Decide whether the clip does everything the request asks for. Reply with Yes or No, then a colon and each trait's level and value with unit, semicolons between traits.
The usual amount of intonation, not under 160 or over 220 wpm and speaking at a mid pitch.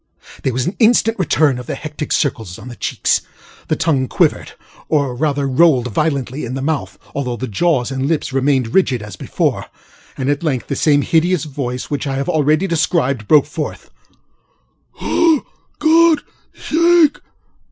Yes: average, 4.1 semitones; average, 165 wpm; medium, 145 Hz